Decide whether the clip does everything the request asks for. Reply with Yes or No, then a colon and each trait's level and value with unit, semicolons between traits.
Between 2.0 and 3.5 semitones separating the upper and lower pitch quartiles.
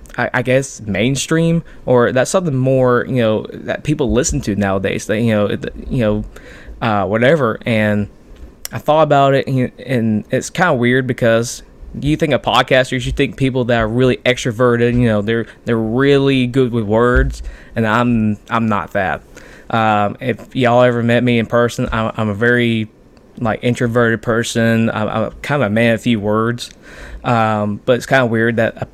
Yes: narrow, 2.5 semitones